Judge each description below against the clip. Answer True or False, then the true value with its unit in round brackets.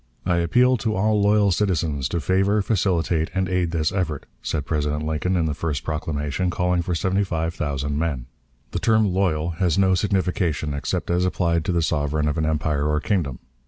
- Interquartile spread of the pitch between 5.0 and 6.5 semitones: False (3.7 semitones)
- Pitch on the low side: True (85 Hz)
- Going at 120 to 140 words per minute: False (190 wpm)